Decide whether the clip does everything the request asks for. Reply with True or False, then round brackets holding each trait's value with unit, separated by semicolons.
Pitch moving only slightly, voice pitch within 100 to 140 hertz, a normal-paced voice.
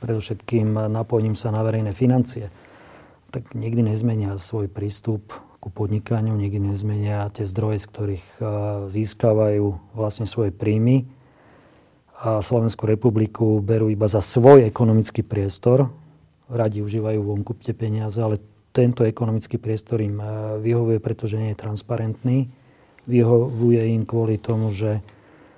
True (1.8 semitones; 110 Hz; 125 wpm)